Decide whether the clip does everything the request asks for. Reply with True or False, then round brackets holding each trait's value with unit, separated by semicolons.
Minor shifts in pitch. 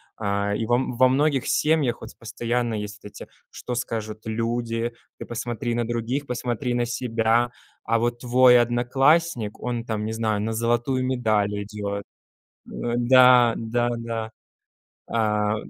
True (1.8 semitones)